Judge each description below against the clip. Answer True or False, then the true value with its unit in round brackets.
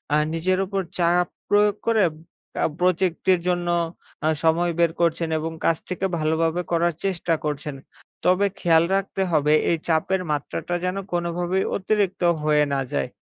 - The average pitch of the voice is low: False (175 Hz)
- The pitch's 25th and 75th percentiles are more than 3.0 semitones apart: False (2.4 semitones)